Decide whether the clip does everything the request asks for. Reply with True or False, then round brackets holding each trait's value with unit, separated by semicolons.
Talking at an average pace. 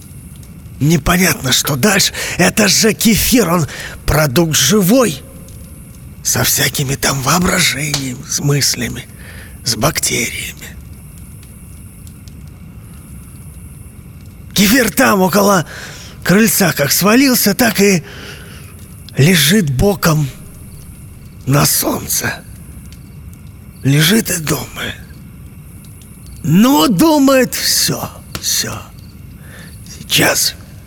False (70 wpm)